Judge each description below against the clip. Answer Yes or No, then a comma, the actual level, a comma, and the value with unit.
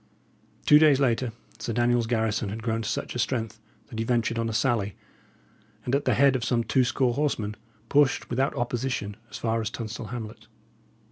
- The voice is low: Yes, low, 120 Hz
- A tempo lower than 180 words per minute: No, average, 190 wpm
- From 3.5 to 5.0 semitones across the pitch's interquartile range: No, narrow, 2.4 semitones